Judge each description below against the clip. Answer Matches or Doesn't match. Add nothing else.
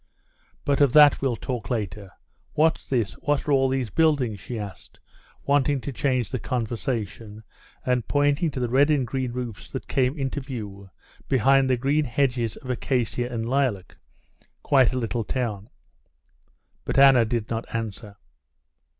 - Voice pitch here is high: Doesn't match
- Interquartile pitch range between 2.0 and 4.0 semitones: Matches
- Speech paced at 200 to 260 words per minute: Doesn't match